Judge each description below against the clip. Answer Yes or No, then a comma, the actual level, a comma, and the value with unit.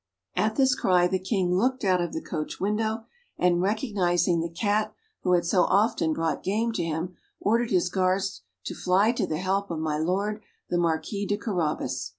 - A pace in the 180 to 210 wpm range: Yes, average, 185 wpm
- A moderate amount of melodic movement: Yes, average, 3.4 semitones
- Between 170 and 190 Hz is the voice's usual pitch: Yes, medium, 185 Hz